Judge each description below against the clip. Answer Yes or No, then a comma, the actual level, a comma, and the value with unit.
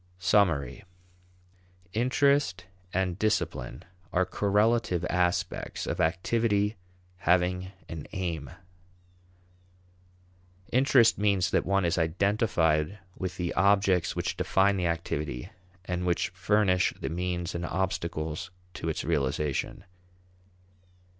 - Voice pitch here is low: Yes, very low, 90 Hz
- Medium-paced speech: No, slow, 100 wpm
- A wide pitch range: No, average, 3.2 semitones